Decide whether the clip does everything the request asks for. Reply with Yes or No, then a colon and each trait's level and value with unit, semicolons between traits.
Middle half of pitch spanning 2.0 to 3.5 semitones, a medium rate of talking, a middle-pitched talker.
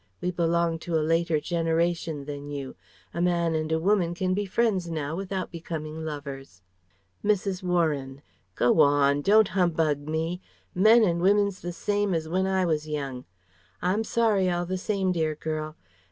Yes: average, 3.2 semitones; average, 165 wpm; medium, 170 Hz